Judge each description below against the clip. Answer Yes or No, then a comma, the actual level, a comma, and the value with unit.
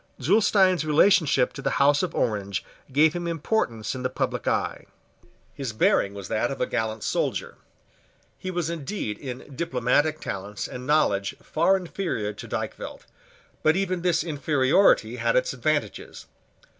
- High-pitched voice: No, medium, 145 Hz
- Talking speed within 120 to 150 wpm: Yes, average, 145 wpm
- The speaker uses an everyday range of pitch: No, wide, 6.1 semitones